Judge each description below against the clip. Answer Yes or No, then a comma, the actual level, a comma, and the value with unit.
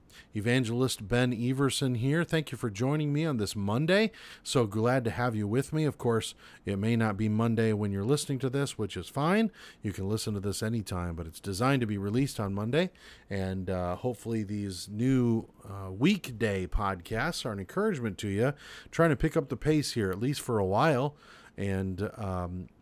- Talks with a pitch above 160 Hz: No, low, 115 Hz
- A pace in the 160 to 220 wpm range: Yes, average, 200 wpm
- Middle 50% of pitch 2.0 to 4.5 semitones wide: No, average, 5.1 semitones